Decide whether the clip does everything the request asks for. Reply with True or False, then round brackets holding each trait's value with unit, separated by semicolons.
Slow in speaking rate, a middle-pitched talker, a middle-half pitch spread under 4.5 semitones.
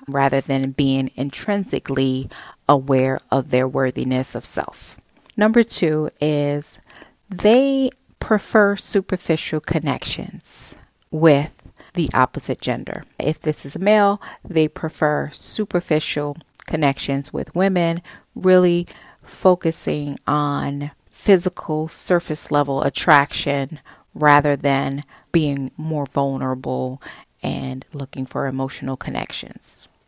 True (100 wpm; 145 Hz; 4.0 semitones)